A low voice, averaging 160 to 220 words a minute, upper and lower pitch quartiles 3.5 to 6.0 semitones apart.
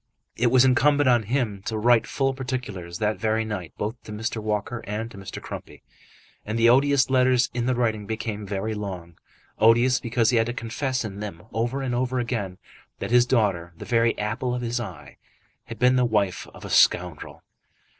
No: low, 115 Hz; average, 195 wpm; average, 3.0 semitones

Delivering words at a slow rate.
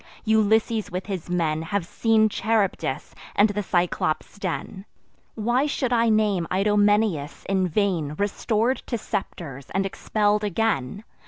Yes: slow, 130 wpm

